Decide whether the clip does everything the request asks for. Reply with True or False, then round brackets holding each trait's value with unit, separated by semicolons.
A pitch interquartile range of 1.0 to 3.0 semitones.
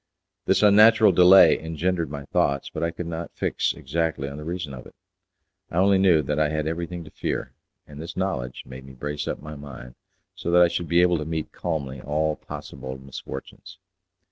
False (3.6 semitones)